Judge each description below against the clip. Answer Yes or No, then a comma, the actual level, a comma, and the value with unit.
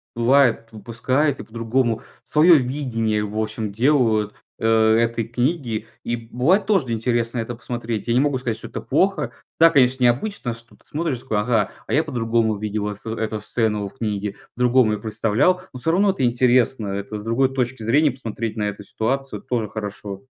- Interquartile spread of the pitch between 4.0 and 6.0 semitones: No, average, 3.1 semitones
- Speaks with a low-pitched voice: Yes, low, 115 Hz